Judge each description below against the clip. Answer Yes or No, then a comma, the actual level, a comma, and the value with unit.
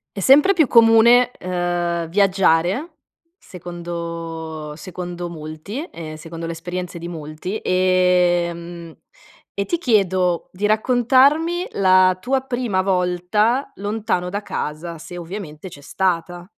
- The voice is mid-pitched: Yes, medium, 180 Hz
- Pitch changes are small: No, average, 3.9 semitones